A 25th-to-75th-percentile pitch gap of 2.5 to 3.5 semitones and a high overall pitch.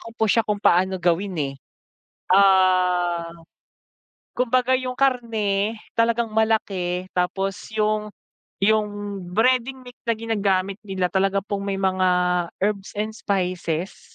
Yes: average, 3.0 semitones; high, 200 Hz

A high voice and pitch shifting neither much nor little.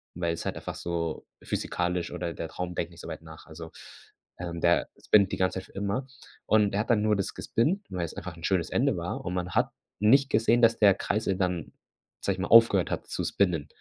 No: very low, 90 Hz; average, 3.8 semitones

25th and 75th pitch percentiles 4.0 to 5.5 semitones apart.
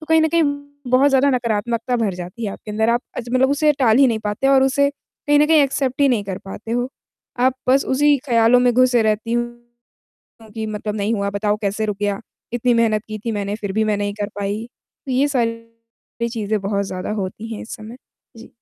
No: average, 3.5 semitones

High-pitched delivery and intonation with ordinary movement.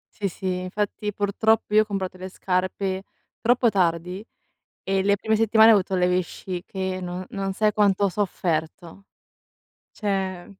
No: high, 195 Hz; narrow, 2.2 semitones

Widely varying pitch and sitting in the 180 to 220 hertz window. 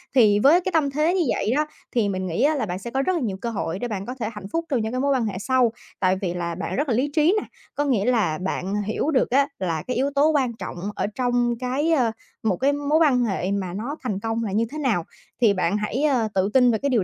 No: wide, 5.7 semitones; high, 240 Hz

